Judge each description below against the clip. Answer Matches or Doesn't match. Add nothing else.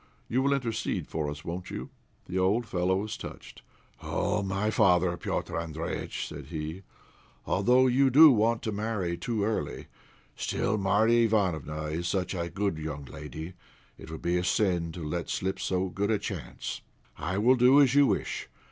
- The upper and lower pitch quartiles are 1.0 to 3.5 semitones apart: Doesn't match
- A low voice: Matches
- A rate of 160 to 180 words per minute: Matches